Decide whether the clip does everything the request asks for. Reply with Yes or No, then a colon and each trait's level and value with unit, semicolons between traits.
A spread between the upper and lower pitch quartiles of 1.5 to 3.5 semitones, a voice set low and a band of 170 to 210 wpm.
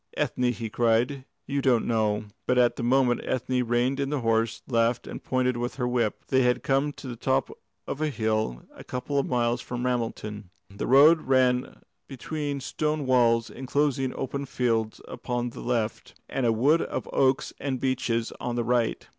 Yes: narrow, 2.4 semitones; low, 125 Hz; average, 185 wpm